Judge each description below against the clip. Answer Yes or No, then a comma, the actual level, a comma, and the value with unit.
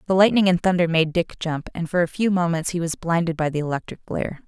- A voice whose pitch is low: No, medium, 170 Hz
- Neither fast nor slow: No, fast, 255 wpm